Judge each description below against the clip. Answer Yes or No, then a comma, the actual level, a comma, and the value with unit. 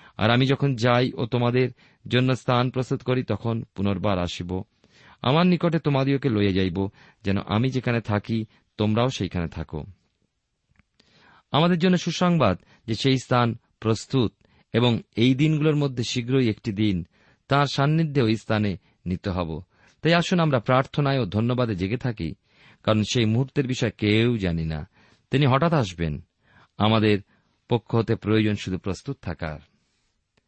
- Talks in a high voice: No, low, 115 Hz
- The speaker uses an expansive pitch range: No, average, 4.7 semitones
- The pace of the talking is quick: Yes, fast, 130 wpm